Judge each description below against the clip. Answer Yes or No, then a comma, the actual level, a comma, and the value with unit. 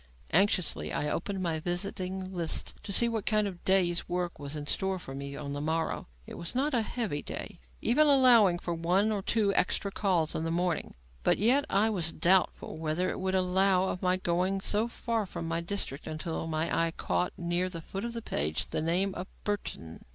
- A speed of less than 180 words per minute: No, fast, 205 wpm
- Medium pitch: Yes, medium, 180 Hz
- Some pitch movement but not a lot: Yes, average, 3.4 semitones